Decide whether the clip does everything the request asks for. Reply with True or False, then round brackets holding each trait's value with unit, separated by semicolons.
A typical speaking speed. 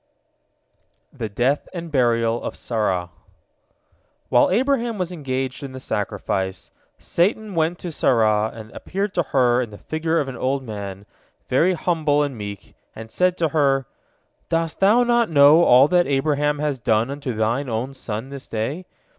True (160 wpm)